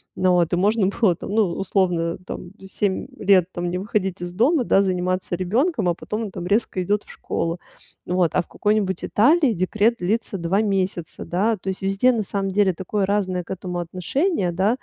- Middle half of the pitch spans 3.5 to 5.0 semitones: No, average, 2.9 semitones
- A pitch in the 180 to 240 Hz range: Yes, high, 190 Hz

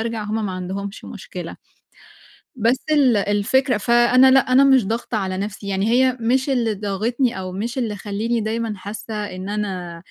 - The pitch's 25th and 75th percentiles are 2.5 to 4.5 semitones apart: Yes, average, 3.3 semitones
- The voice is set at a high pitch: Yes, high, 220 Hz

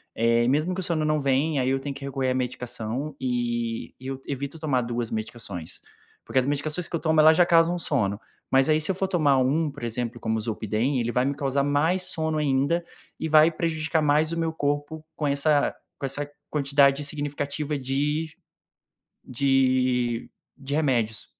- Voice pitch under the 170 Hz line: Yes, medium, 140 Hz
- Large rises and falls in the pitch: No, average, 3.4 semitones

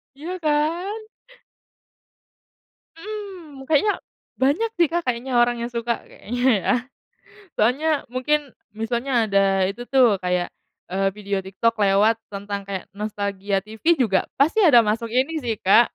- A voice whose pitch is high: Yes, high, 240 Hz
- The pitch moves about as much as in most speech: No, wide, 6.4 semitones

